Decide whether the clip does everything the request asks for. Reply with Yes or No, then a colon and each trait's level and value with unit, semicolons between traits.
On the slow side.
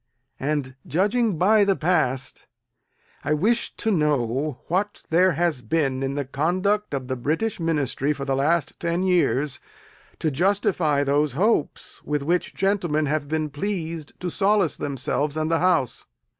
No: average, 150 wpm